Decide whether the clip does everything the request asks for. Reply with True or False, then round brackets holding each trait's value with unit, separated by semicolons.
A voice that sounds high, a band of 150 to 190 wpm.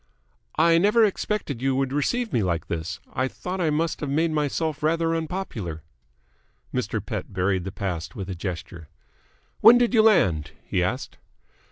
False (140 Hz; 165 wpm)